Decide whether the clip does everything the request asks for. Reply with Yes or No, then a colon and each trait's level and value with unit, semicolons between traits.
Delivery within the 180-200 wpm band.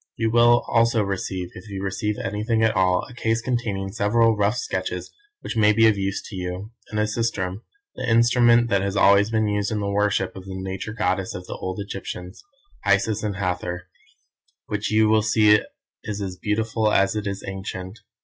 Yes: average, 190 wpm